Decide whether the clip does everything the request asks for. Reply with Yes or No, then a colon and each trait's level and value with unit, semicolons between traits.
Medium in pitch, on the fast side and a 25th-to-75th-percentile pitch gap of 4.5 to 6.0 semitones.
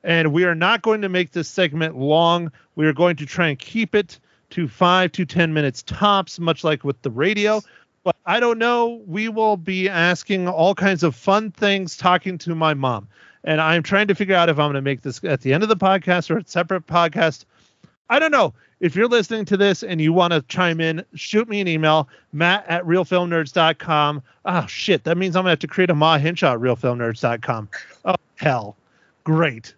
No: medium, 170 Hz; fast, 215 wpm; average, 3.8 semitones